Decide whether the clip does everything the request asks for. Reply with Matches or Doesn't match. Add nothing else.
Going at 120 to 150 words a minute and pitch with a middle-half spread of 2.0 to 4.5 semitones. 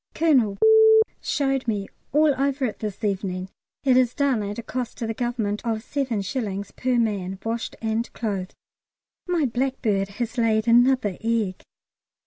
Matches